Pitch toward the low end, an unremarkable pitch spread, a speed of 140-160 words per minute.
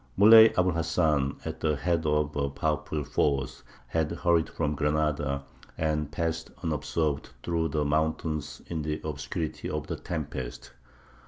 No: very low, 75 Hz; narrow, 1.8 semitones; average, 145 wpm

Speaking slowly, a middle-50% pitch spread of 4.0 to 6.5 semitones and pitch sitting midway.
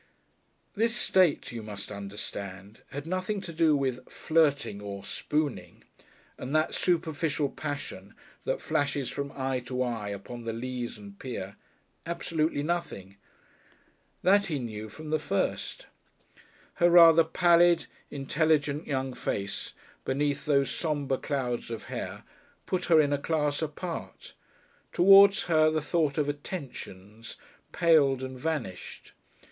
Yes: slow, 130 wpm; average, 5.1 semitones; medium, 145 Hz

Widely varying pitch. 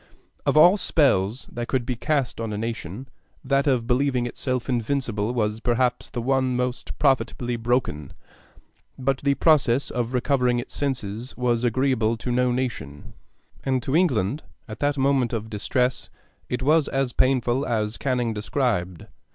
No: average, 2.7 semitones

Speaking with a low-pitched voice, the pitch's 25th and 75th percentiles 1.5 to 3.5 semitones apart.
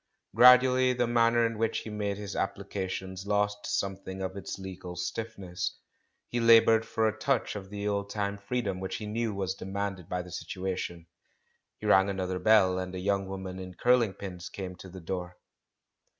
Yes: low, 100 Hz; average, 2.8 semitones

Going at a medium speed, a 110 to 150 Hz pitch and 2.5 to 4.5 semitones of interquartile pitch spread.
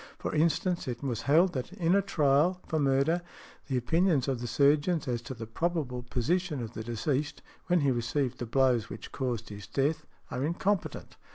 No: average, 185 wpm; medium, 140 Hz; average, 5.2 semitones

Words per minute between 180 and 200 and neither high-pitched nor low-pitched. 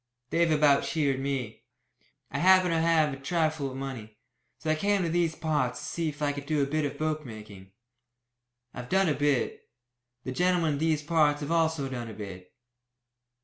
Yes: average, 190 wpm; medium, 150 Hz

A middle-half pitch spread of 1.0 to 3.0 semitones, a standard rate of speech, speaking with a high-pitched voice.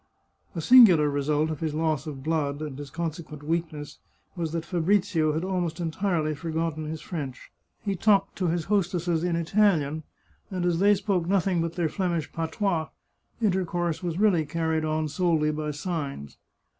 No: average, 2.7 semitones; average, 170 wpm; medium, 165 Hz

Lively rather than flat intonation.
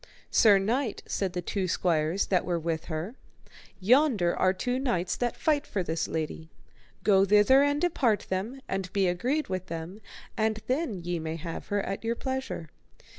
Yes: wide, 5.8 semitones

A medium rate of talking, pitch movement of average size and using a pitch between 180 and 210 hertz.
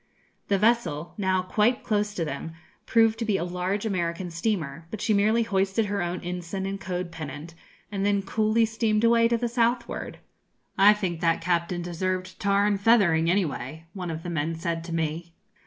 Yes: average, 185 wpm; average, 4.0 semitones; high, 190 Hz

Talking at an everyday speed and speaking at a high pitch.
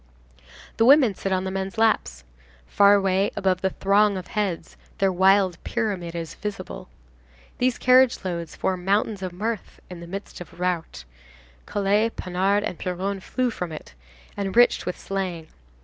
Yes: average, 160 wpm; high, 195 Hz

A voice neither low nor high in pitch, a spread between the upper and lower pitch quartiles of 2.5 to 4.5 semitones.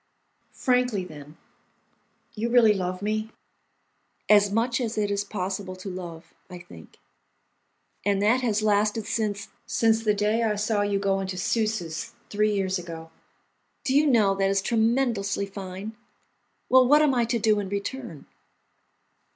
No: high, 205 Hz; average, 2.8 semitones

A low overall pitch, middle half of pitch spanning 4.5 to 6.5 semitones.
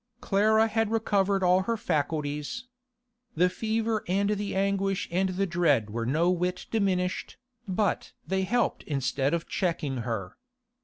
No: medium, 185 Hz; average, 4.8 semitones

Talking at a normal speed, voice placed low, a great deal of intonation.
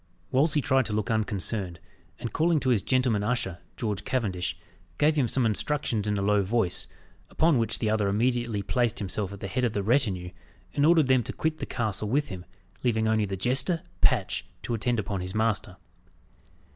No: average, 190 wpm; low, 110 Hz; average, 4.1 semitones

